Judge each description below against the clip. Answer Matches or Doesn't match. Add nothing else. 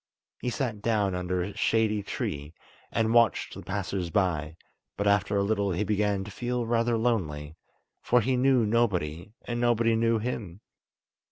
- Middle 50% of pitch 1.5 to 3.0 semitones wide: Doesn't match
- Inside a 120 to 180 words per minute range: Matches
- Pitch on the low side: Matches